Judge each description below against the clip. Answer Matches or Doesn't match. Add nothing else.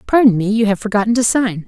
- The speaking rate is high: Matches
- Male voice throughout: Doesn't match